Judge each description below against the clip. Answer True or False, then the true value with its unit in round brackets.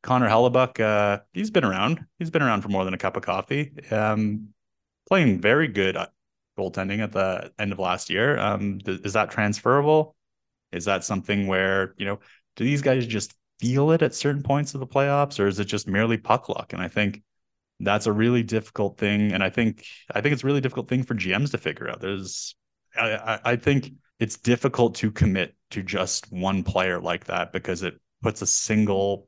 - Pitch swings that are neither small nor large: True (4.2 semitones)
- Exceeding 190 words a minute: True (205 wpm)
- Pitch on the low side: True (105 Hz)